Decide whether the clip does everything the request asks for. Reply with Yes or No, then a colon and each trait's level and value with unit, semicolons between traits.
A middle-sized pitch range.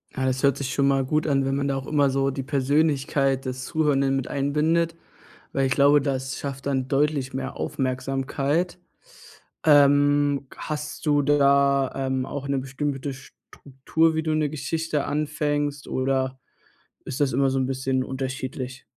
No: narrow, 1.6 semitones